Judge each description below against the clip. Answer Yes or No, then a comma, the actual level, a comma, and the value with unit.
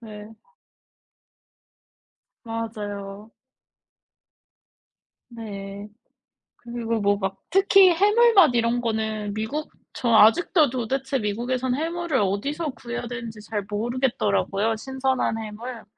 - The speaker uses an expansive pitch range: No, average, 4.0 semitones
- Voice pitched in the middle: No, high, 230 Hz